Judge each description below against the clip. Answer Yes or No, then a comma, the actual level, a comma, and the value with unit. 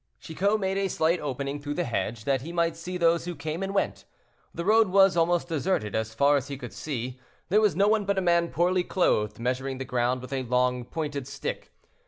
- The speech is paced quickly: Yes, fast, 225 wpm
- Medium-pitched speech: Yes, medium, 160 Hz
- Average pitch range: No, wide, 5.9 semitones